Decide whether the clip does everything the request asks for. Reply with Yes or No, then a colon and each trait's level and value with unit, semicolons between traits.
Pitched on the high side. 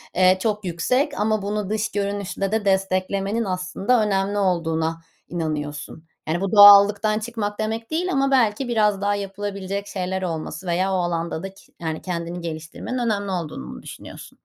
Yes: high, 195 Hz